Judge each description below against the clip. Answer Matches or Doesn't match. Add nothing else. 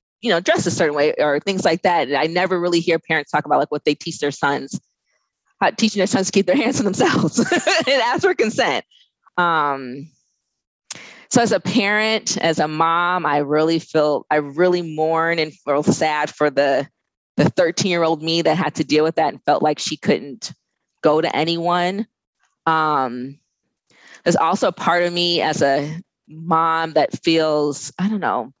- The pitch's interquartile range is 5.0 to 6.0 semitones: Doesn't match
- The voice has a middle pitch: Matches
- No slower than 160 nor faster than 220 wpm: Matches